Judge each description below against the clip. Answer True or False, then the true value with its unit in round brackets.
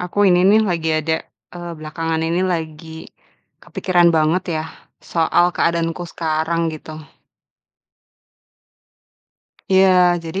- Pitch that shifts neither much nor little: False (1.6 semitones)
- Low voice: False (165 Hz)